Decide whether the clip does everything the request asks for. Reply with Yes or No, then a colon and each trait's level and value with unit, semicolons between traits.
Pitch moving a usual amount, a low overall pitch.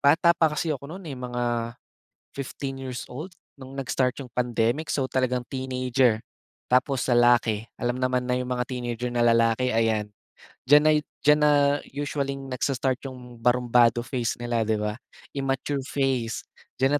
No: narrow, 2.2 semitones; low, 125 Hz